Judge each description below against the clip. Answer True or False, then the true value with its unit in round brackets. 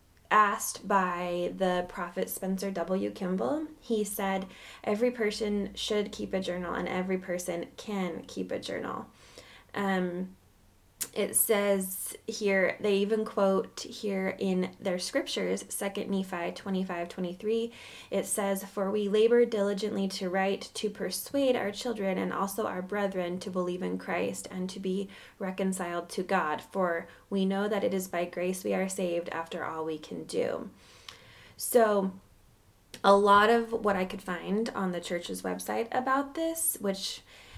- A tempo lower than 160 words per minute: True (150 wpm)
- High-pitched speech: True (195 Hz)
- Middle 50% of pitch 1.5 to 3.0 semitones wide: True (2.6 semitones)